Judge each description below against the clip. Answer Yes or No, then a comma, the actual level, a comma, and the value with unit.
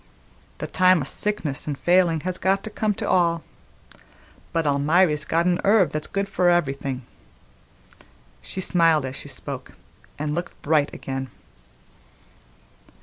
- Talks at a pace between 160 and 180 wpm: No, average, 140 wpm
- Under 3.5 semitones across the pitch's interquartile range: No, average, 4.0 semitones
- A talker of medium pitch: Yes, medium, 165 Hz